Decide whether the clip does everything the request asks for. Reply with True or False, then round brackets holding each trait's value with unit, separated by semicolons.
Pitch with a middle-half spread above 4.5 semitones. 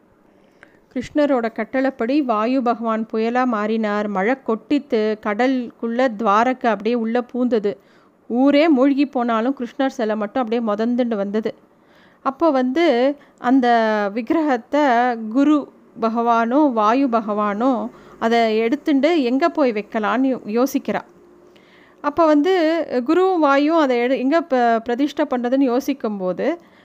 False (3.7 semitones)